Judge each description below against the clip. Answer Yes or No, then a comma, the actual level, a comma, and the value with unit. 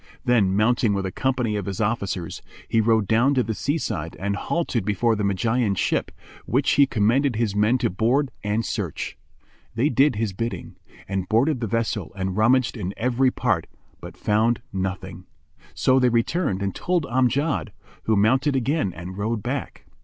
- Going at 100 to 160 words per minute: No, average, 175 wpm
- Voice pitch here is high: No, low, 115 Hz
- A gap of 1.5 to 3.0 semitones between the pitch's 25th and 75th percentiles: No, average, 4.3 semitones